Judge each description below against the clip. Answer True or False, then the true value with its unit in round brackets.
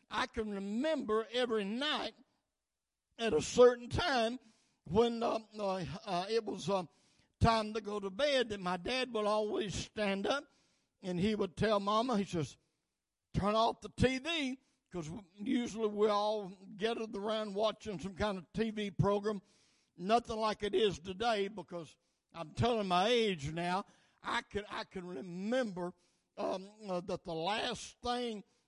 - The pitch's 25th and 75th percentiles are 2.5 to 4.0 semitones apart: True (3.2 semitones)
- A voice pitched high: True (210 Hz)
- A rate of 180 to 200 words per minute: False (155 wpm)